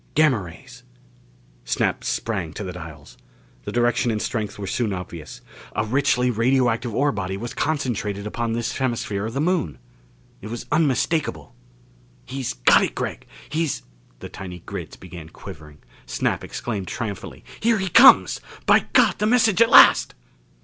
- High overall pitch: No, low, 115 Hz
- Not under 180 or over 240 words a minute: No, average, 155 wpm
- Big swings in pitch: Yes, wide, 6.1 semitones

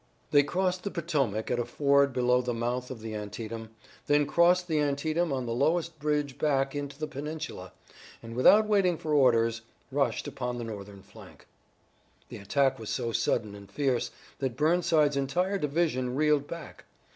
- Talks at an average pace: Yes, average, 170 wpm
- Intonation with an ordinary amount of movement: Yes, average, 4.3 semitones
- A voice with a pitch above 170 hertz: No, medium, 140 Hz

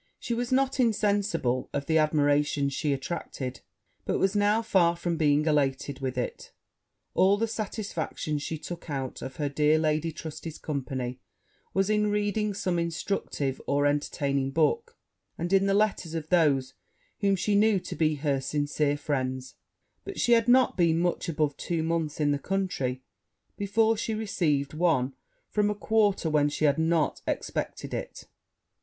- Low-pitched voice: No, medium, 160 Hz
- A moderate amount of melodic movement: No, wide, 5.9 semitones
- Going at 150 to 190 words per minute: Yes, average, 160 wpm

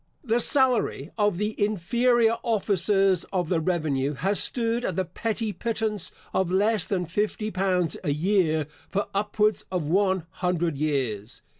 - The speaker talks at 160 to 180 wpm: No, average, 145 wpm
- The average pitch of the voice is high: Yes, high, 195 Hz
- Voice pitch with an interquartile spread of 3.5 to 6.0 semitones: Yes, average, 4.2 semitones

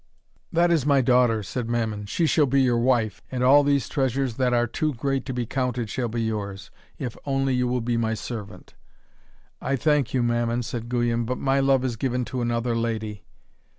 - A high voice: No, low, 125 Hz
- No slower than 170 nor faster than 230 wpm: Yes, average, 200 wpm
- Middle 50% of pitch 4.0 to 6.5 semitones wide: No, narrow, 2.5 semitones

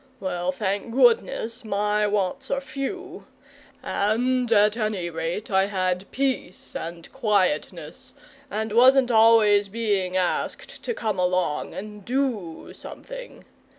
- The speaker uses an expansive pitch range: No, average, 4.6 semitones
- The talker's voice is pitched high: Yes, high, 210 Hz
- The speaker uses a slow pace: Yes, slow, 120 wpm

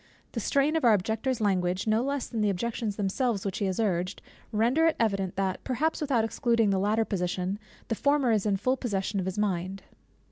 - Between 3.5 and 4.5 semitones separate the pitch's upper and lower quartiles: Yes, average, 3.9 semitones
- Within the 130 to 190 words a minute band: No, fast, 205 wpm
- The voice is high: Yes, high, 215 Hz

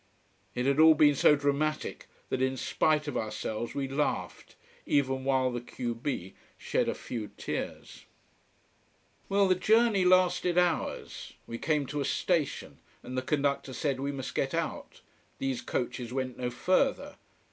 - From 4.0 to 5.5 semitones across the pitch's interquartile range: No, average, 3.5 semitones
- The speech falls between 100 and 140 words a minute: No, average, 155 wpm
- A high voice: No, medium, 140 Hz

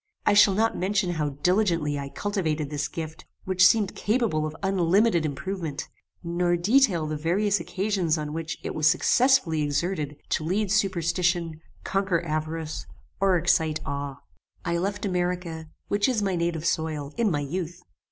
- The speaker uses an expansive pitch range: No, average, 3.9 semitones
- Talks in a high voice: No, medium, 175 Hz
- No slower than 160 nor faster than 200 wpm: No, average, 150 wpm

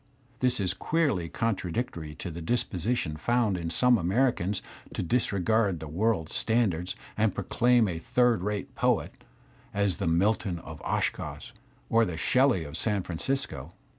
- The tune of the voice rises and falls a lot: Yes, wide, 5.7 semitones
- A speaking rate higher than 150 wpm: No, average, 140 wpm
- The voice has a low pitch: Yes, low, 100 Hz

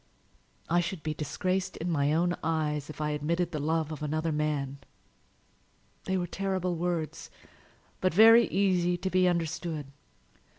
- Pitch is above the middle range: No, medium, 165 Hz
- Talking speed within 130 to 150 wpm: Yes, average, 145 wpm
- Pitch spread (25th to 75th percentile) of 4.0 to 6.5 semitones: No, average, 3.1 semitones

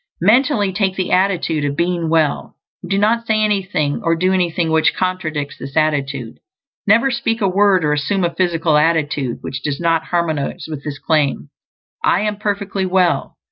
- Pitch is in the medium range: Yes, medium, 170 Hz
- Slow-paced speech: No, average, 175 wpm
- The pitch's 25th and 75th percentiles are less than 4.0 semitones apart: No, average, 4.3 semitones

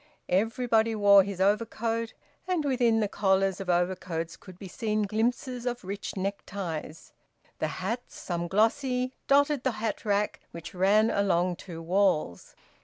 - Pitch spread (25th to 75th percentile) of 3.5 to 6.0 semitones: Yes, average, 3.8 semitones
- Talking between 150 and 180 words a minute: No, average, 140 wpm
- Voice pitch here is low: No, high, 205 Hz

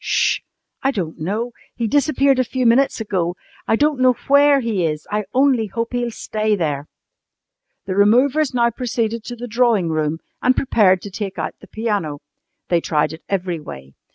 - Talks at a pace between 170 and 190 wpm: Yes, average, 180 wpm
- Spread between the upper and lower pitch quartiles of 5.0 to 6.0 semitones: Yes, wide, 5.6 semitones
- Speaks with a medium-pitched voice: No, high, 220 Hz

